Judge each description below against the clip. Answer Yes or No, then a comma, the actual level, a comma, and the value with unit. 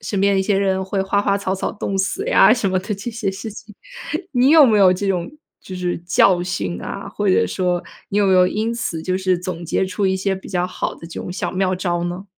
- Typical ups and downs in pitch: No, narrow, 1.9 semitones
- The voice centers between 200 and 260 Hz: No, high, 190 Hz